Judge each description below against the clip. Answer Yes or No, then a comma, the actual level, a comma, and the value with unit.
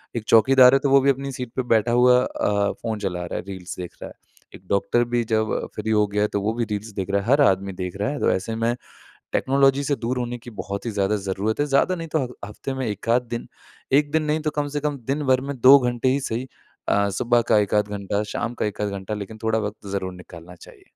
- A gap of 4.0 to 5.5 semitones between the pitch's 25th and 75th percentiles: Yes, average, 4.4 semitones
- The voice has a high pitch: No, low, 115 Hz